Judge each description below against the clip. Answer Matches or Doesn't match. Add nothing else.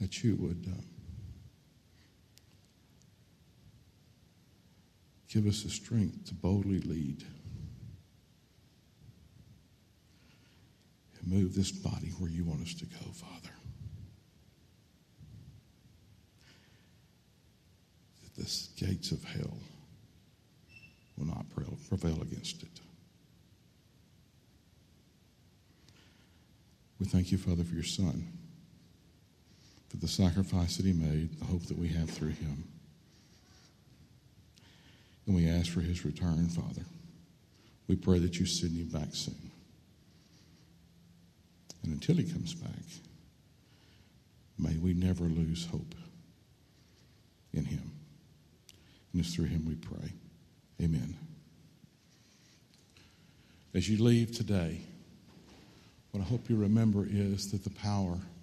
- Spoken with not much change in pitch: Doesn't match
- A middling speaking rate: Doesn't match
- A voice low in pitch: Matches